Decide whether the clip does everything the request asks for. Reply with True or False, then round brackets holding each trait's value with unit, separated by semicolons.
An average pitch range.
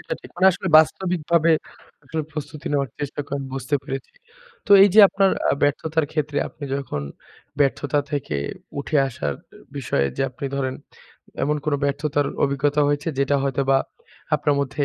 False (1.9 semitones)